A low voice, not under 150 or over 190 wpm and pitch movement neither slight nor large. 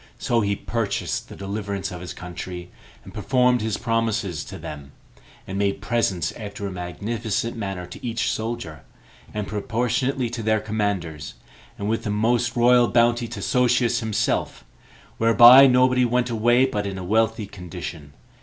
Yes: low, 110 Hz; average, 155 wpm; average, 3.3 semitones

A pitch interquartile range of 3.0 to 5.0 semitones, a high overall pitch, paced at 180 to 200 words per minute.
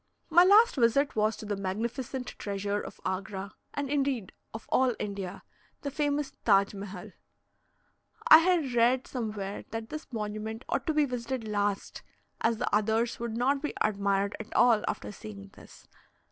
No: average, 4.7 semitones; high, 225 Hz; average, 160 wpm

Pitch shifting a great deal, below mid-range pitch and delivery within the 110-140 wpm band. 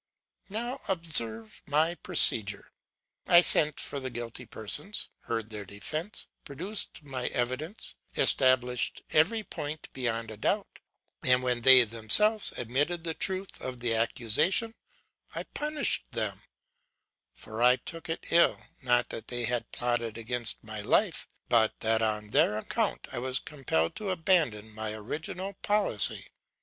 Yes: wide, 6.6 semitones; low, 125 Hz; slow, 135 wpm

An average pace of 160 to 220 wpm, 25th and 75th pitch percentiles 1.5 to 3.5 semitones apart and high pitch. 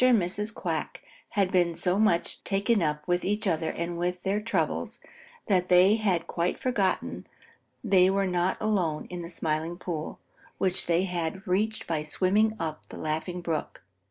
No: average, 165 wpm; average, 2.9 semitones; medium, 180 Hz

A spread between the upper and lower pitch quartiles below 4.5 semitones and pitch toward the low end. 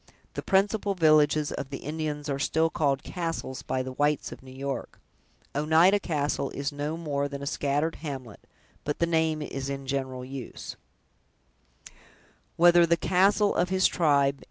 No: narrow, 2.6 semitones; medium, 145 Hz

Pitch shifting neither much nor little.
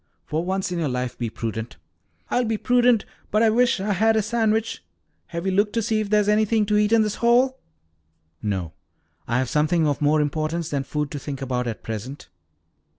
No: wide, 7.5 semitones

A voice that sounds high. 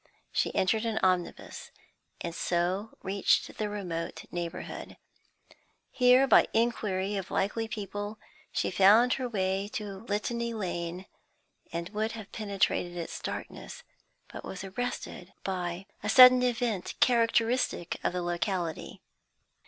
Yes: high, 200 Hz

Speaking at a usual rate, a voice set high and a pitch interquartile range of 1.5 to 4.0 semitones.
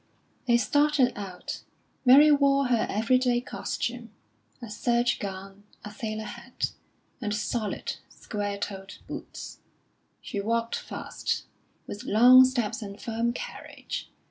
No: slow, 120 wpm; high, 230 Hz; average, 3.3 semitones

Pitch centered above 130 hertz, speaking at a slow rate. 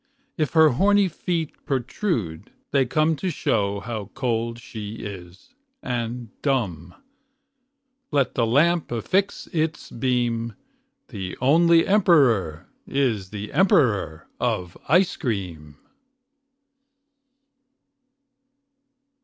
No: low, 120 Hz; slow, 95 wpm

